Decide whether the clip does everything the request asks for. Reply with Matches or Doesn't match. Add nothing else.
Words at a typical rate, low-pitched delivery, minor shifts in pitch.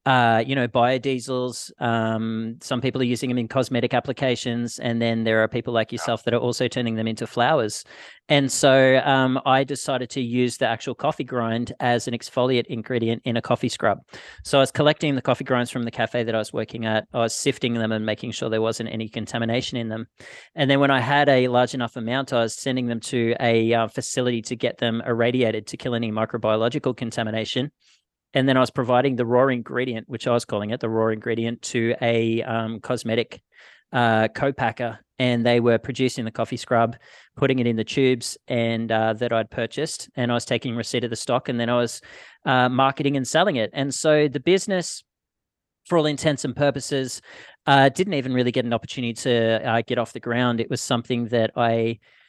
Doesn't match